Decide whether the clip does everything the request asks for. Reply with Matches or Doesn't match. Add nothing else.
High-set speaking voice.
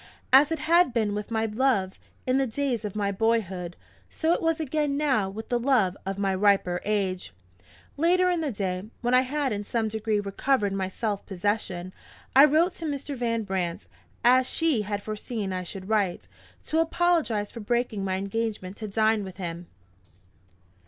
Matches